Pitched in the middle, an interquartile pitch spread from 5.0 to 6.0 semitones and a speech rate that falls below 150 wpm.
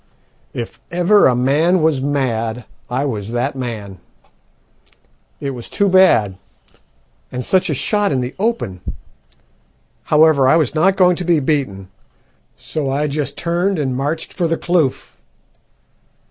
Yes: medium, 145 Hz; wide, 5.5 semitones; average, 140 wpm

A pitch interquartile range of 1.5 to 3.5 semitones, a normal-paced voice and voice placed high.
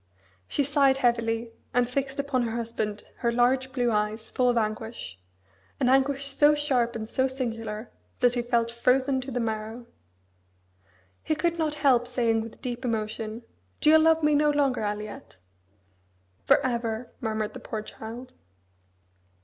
Yes: average, 3.1 semitones; average, 155 wpm; high, 245 Hz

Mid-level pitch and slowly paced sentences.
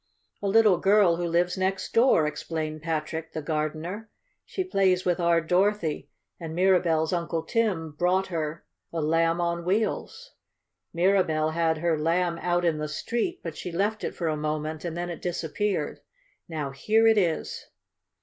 No: medium, 170 Hz; average, 160 wpm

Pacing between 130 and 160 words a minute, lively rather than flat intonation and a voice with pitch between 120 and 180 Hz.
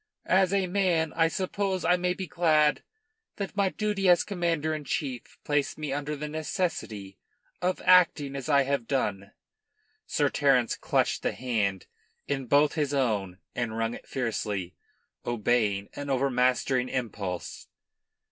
Yes: average, 145 wpm; wide, 6.3 semitones; medium, 140 Hz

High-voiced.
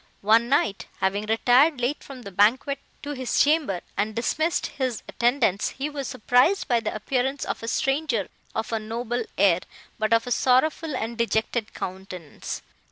Yes: high, 240 Hz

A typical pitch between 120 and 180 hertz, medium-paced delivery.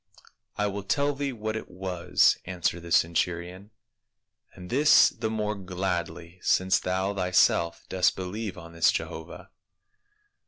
No: very low, 95 Hz; average, 150 wpm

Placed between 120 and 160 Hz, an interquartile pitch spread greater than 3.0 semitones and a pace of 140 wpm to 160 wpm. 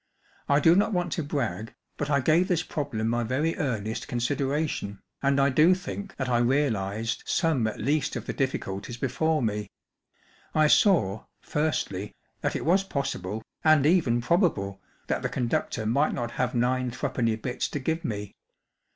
No: low, 135 Hz; wide, 5.5 semitones; average, 170 wpm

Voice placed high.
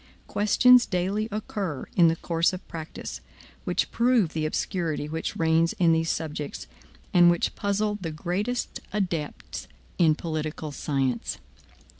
No: medium, 170 Hz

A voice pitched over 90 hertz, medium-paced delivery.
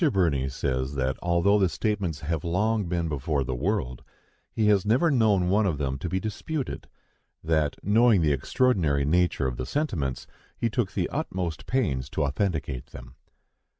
No: very low, 85 Hz; average, 165 wpm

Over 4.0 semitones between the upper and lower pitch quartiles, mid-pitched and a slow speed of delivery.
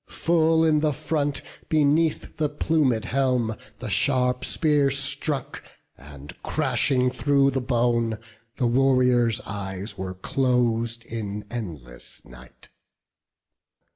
No: average, 4.4 semitones; low, 125 Hz; slow, 105 wpm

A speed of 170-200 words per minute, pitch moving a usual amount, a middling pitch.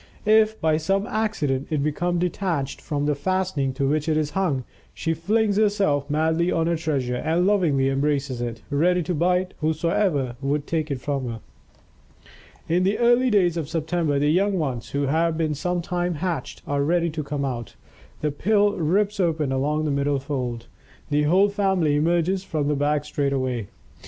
Yes: average, 175 wpm; average, 4.1 semitones; medium, 155 Hz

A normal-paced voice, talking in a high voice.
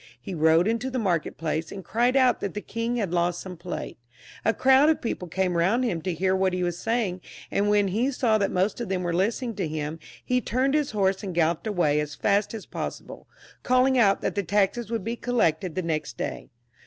No: fast, 230 wpm; high, 195 Hz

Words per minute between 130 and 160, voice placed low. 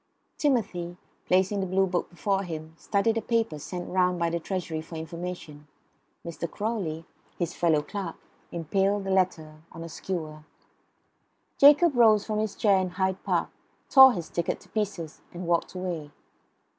No: average, 155 wpm; medium, 180 Hz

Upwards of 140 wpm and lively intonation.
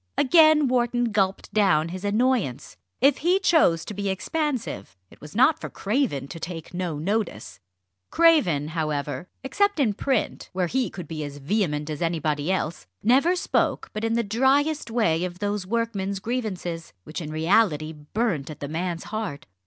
Yes: average, 165 wpm; wide, 7.3 semitones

